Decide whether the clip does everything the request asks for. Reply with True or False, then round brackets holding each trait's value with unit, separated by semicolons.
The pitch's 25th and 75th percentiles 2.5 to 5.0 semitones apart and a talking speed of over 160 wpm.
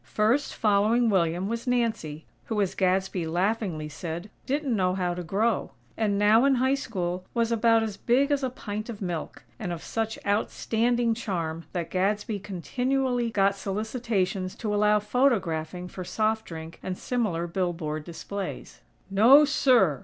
False (4.5 semitones; 155 wpm)